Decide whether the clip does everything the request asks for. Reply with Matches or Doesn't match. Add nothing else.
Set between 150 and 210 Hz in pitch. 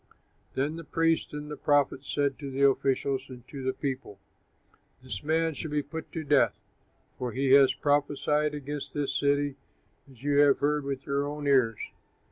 Doesn't match